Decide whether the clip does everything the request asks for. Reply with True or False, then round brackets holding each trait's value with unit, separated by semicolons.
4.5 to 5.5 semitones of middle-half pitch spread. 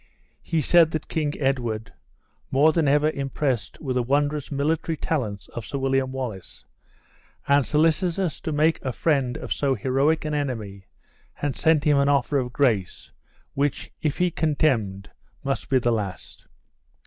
False (3.5 semitones)